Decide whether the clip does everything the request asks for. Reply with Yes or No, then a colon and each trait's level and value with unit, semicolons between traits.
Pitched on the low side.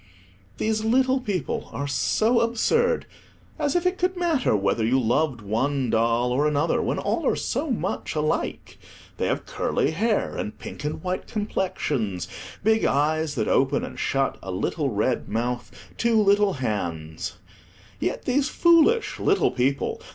No: medium, 150 Hz